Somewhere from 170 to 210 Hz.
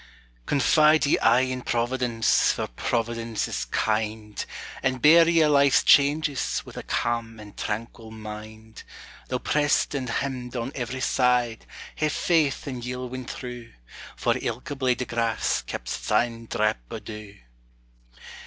No: low, 120 Hz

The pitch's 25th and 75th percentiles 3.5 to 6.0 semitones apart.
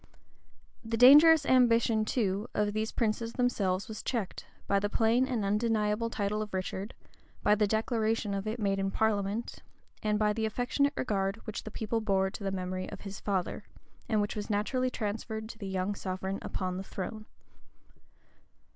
No: narrow, 2.5 semitones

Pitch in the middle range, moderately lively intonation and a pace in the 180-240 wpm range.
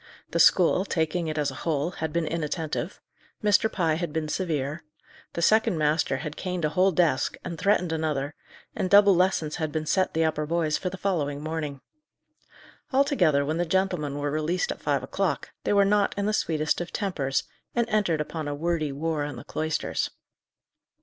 Yes: medium, 160 Hz; average, 3.4 semitones; average, 185 wpm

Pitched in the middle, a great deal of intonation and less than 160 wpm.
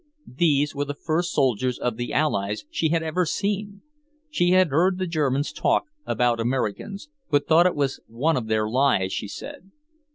No: medium, 145 Hz; wide, 6.0 semitones; average, 175 wpm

